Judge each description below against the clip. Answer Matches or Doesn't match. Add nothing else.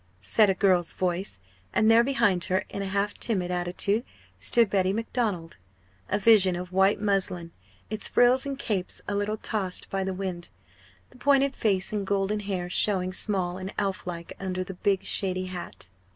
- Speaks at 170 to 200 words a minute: Matches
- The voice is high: Matches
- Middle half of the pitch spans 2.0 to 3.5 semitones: Matches